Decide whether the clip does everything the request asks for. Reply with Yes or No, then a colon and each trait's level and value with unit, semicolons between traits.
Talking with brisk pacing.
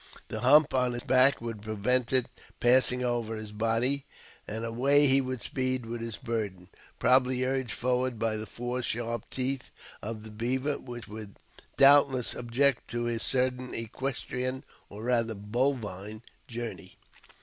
No: average, 150 wpm